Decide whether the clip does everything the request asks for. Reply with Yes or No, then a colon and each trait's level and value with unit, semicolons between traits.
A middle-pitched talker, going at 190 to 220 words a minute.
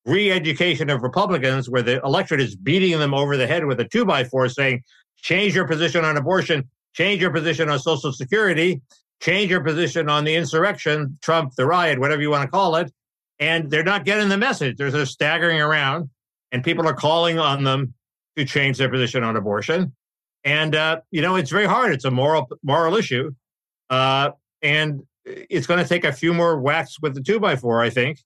Yes: medium, 155 Hz; average, 200 wpm